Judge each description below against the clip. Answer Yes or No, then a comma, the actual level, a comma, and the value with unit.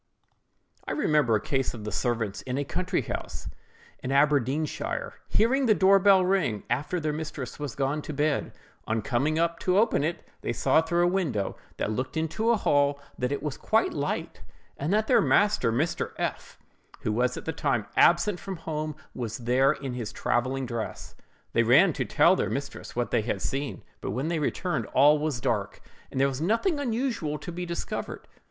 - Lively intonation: Yes, wide, 5.7 semitones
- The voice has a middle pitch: Yes, medium, 150 Hz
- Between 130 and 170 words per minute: No, average, 190 wpm